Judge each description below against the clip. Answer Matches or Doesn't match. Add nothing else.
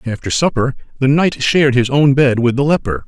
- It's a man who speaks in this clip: Matches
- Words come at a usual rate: Doesn't match